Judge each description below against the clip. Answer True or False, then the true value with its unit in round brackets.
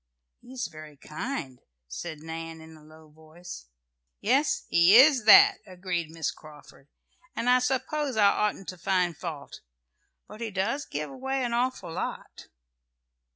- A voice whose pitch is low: False (185 Hz)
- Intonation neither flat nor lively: False (7.9 semitones)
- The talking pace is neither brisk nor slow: True (150 wpm)